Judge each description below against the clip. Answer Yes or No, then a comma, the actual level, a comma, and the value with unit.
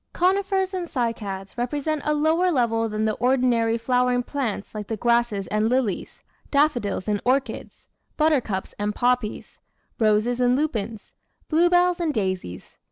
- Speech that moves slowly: Yes, slow, 130 wpm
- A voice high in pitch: Yes, high, 245 Hz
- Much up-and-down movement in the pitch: Yes, wide, 5.8 semitones